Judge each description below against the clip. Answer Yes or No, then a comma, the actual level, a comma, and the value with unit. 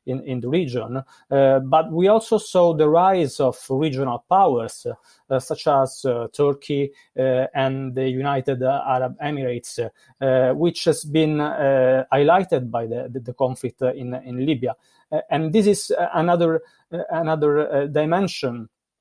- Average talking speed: Yes, average, 145 wpm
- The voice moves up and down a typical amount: Yes, average, 3.6 semitones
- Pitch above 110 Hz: Yes, low, 135 Hz